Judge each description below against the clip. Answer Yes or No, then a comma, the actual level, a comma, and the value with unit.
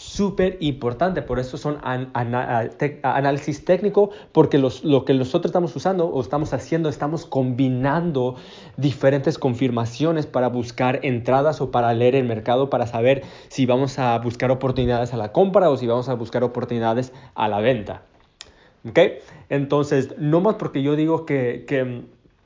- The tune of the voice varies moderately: Yes, average, 3.4 semitones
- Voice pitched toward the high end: No, low, 135 Hz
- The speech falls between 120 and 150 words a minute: No, average, 165 wpm